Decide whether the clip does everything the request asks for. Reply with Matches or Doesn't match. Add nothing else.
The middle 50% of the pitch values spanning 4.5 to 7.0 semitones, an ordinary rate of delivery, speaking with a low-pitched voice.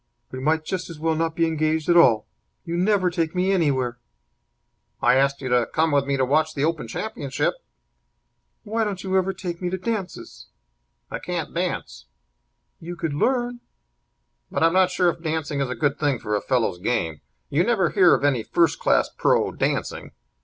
Doesn't match